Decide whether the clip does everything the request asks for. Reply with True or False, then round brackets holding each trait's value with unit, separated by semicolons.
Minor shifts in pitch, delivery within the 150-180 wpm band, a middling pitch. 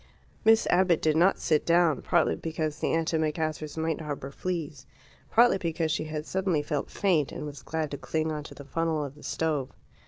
False (1.8 semitones; 190 wpm; 160 Hz)